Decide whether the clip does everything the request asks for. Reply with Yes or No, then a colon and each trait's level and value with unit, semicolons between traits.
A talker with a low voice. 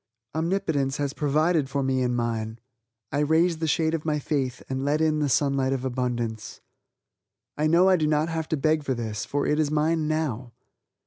No: medium, 145 Hz